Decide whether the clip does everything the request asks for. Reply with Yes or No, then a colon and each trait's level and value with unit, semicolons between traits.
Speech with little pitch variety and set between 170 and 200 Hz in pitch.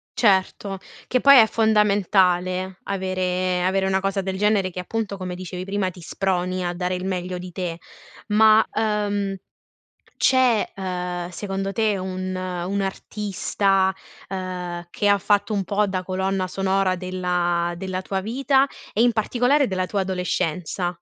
Yes: narrow, 2.0 semitones; high, 190 Hz